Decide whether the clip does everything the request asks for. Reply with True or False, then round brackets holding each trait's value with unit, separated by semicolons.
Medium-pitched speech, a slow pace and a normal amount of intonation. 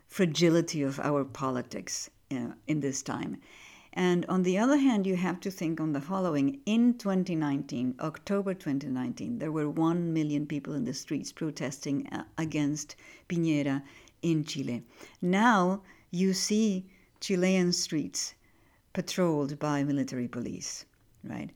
True (165 Hz; 130 wpm; 4.6 semitones)